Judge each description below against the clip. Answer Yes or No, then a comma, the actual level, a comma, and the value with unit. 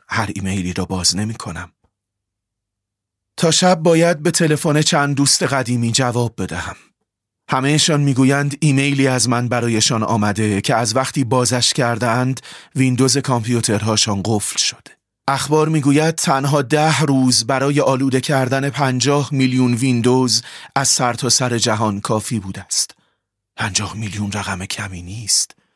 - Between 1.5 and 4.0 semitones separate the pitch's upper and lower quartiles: No, average, 5.0 semitones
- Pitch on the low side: Yes, low, 125 Hz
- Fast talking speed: No, average, 130 wpm